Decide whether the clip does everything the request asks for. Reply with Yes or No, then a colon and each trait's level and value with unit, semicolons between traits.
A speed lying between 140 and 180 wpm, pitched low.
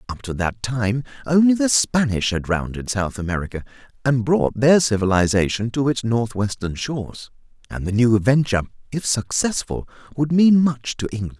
Yes: average, 160 wpm; low, 120 Hz